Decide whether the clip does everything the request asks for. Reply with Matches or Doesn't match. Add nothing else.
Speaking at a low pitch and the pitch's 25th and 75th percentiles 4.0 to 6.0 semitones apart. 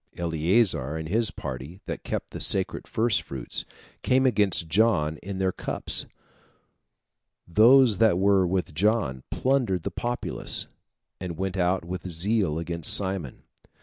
Matches